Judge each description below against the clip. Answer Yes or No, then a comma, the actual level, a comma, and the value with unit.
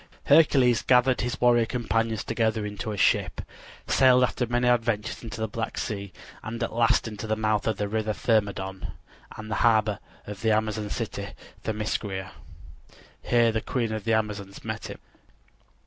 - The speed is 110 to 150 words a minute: No, average, 165 wpm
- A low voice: Yes, low, 110 Hz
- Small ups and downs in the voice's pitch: Yes, narrow, 2.0 semitones